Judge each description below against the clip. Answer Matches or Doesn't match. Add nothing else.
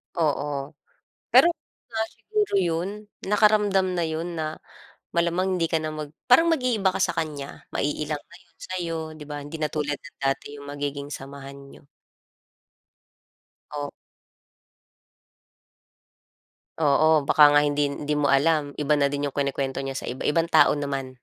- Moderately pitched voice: Matches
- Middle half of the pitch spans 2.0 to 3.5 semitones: Matches